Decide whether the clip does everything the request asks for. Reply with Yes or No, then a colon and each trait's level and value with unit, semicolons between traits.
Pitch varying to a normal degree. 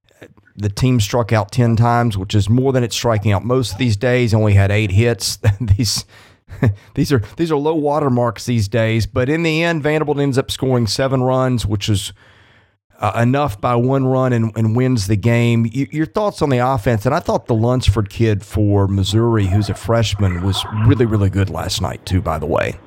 Yes: average, 3.6 semitones